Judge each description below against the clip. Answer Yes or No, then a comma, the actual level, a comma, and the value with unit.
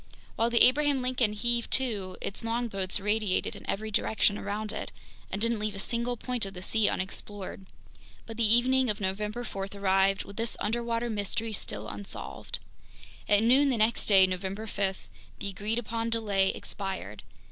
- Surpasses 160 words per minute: Yes, average, 170 wpm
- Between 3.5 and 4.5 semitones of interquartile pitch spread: No, average, 3.0 semitones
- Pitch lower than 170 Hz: No, high, 215 Hz